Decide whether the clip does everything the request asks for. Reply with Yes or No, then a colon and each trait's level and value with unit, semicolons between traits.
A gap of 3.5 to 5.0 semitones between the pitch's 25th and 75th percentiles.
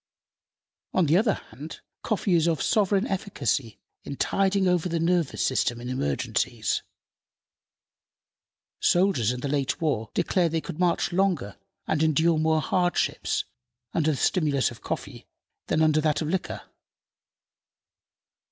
Yes: average, 4.4 semitones